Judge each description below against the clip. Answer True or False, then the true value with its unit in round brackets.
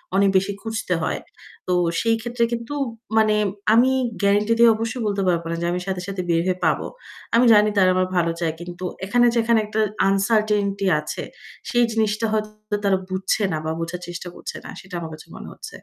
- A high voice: True (200 Hz)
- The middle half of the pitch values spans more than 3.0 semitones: True (3.5 semitones)